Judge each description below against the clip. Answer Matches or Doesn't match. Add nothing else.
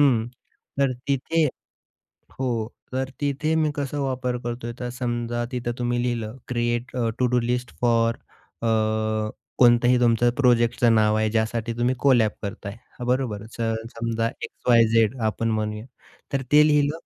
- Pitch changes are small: Matches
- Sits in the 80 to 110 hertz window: Doesn't match